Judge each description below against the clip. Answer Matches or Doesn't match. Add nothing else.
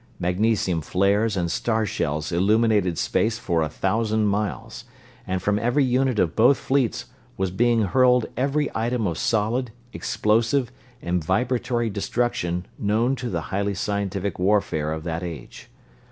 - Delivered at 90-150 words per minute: Matches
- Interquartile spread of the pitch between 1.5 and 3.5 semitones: Doesn't match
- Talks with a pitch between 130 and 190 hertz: Doesn't match